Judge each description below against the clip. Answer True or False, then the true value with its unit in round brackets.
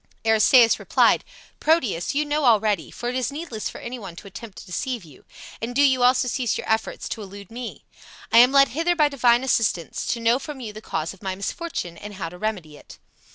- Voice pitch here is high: True (230 Hz)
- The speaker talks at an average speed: False (220 wpm)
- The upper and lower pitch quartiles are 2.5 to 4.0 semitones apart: False (4.7 semitones)